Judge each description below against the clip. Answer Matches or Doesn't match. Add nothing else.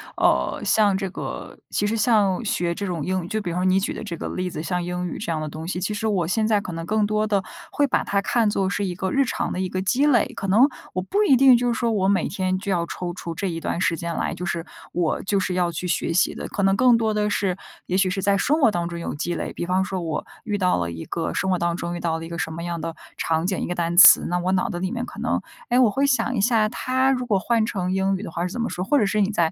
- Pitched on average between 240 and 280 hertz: Doesn't match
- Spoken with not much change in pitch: Doesn't match